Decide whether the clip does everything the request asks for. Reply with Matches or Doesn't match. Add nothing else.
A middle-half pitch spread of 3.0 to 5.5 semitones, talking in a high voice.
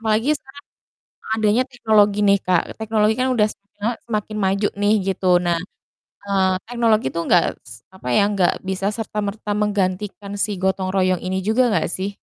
Doesn't match